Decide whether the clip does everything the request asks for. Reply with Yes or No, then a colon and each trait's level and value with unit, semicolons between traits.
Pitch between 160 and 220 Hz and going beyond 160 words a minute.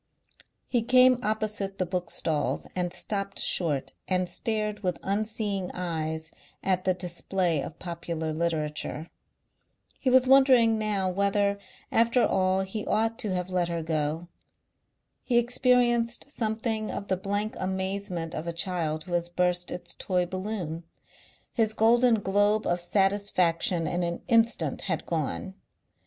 No: high, 190 Hz; slow, 135 wpm